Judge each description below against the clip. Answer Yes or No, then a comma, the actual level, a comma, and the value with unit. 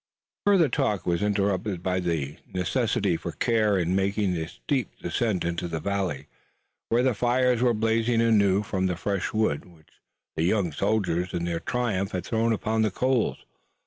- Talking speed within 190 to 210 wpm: No, average, 170 wpm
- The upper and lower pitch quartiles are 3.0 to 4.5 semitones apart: Yes, average, 4.2 semitones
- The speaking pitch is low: Yes, low, 100 Hz